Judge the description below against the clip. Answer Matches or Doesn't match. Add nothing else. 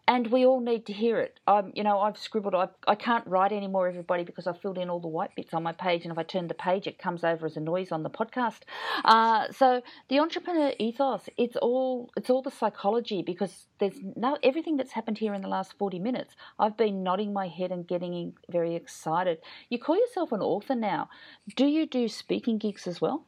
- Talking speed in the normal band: Doesn't match